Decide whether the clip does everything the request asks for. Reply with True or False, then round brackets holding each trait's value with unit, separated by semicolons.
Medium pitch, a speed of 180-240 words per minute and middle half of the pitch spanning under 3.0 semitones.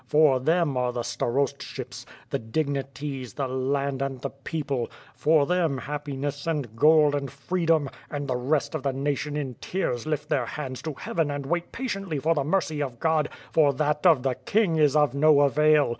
True (145 Hz; 185 wpm; 2.5 semitones)